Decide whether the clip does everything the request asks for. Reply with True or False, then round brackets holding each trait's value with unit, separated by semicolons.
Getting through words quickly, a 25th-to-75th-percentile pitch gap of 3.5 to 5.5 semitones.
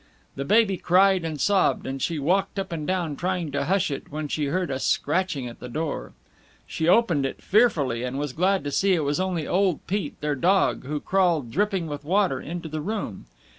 True (210 wpm; 4.7 semitones)